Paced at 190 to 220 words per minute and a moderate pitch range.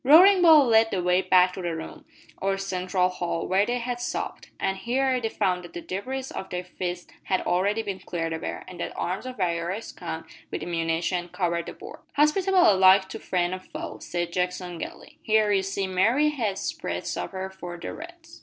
Yes: average, 200 wpm; average, 4.3 semitones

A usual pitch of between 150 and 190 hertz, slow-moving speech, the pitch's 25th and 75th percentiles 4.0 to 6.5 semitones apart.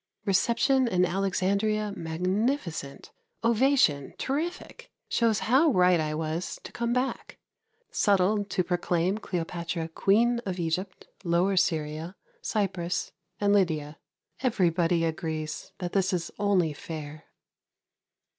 Yes: medium, 185 Hz; slow, 110 wpm; average, 4.3 semitones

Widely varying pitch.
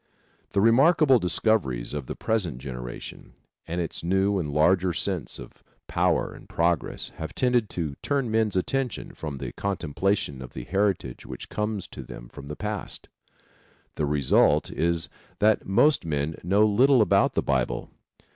Yes: wide, 6.5 semitones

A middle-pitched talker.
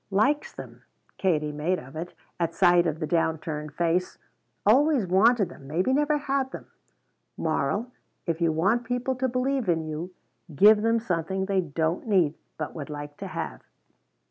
Yes: medium, 180 Hz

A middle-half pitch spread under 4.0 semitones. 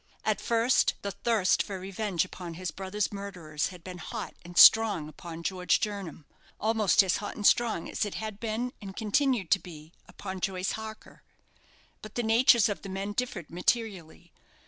Yes: average, 3.4 semitones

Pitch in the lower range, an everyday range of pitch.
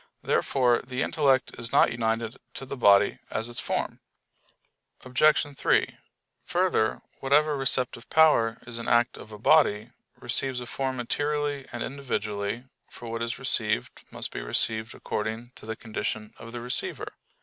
Yes: low, 120 Hz; average, 3.1 semitones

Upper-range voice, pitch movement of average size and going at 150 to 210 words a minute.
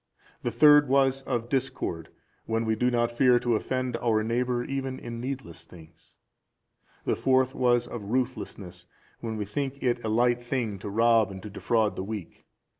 No: low, 120 Hz; average, 3.0 semitones; average, 175 wpm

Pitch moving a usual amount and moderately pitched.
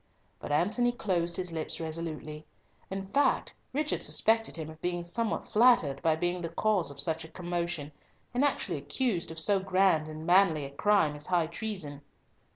Yes: average, 4.2 semitones; medium, 175 Hz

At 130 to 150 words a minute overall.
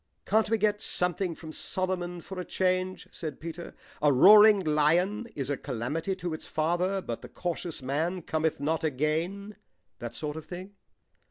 No: average, 165 wpm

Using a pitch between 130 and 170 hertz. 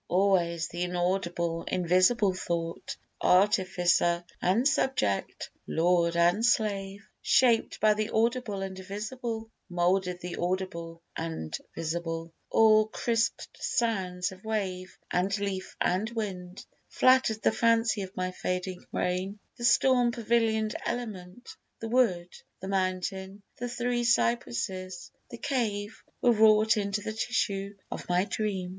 No: high, 195 Hz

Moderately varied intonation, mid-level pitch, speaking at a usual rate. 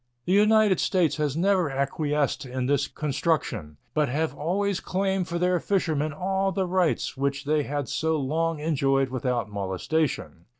Yes: average, 4.8 semitones; medium, 155 Hz; average, 155 wpm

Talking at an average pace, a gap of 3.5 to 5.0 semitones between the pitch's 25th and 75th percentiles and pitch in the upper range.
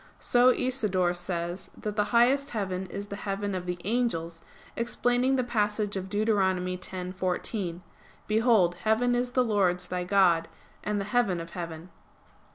Yes: average, 150 wpm; average, 4.2 semitones; high, 200 Hz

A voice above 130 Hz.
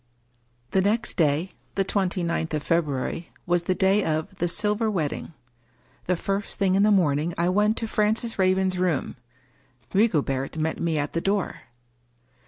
Yes: medium, 185 Hz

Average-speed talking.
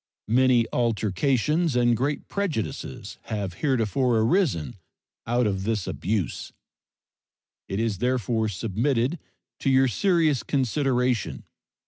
No: slow, 100 wpm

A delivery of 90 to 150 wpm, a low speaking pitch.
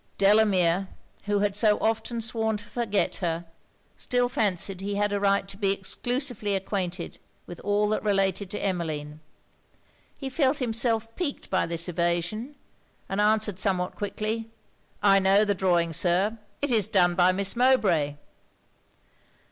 No: average, 145 wpm; high, 200 Hz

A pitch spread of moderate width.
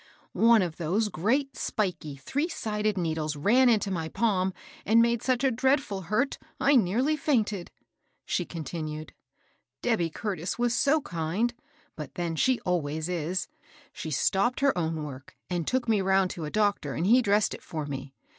No: wide, 6.5 semitones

